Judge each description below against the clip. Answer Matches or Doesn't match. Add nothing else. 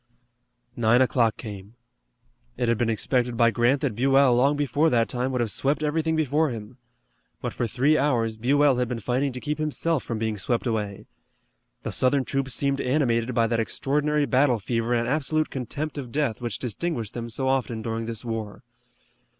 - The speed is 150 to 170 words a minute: Doesn't match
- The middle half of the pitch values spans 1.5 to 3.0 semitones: Doesn't match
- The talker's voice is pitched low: Matches